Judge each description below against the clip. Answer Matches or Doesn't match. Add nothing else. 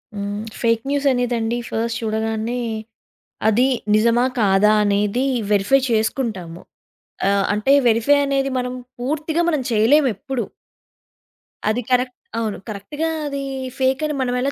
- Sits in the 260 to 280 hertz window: Doesn't match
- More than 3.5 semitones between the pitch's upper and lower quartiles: Matches